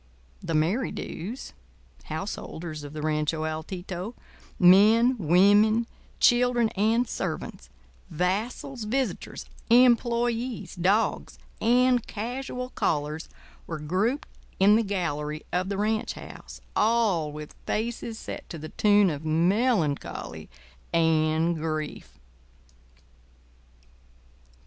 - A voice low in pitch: No, high, 195 Hz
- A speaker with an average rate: No, slow, 95 wpm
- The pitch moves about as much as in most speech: No, wide, 6.5 semitones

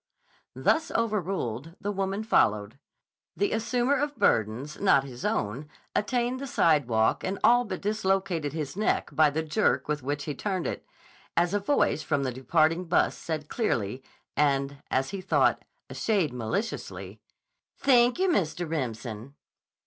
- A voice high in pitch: No, medium, 165 Hz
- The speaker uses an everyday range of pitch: No, wide, 7.2 semitones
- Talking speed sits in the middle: Yes, average, 150 wpm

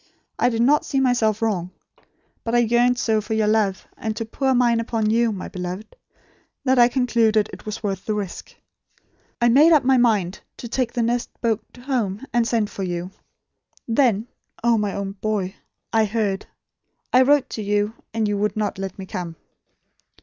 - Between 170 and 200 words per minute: Yes, average, 185 wpm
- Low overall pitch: No, high, 220 Hz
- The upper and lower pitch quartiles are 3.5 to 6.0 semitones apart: No, average, 2.8 semitones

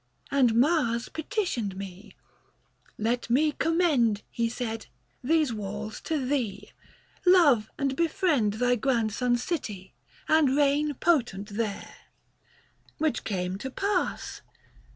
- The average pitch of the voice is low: No, high, 245 Hz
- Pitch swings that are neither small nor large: No, wide, 5.8 semitones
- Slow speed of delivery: Yes, slow, 115 wpm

